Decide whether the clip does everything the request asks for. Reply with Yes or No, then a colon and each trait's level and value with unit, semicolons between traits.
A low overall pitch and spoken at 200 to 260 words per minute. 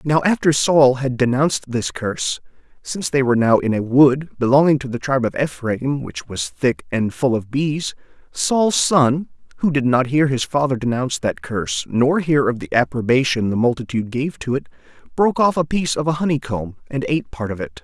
Yes: low, 130 Hz; fast, 205 wpm